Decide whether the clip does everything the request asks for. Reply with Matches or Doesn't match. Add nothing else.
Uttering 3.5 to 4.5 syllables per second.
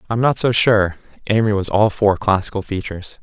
Doesn't match